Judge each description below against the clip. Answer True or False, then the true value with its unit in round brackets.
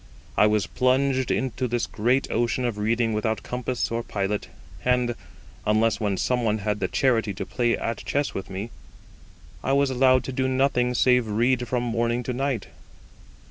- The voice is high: False (120 Hz)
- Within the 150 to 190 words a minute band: True (175 wpm)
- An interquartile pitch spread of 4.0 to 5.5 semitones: False (2.8 semitones)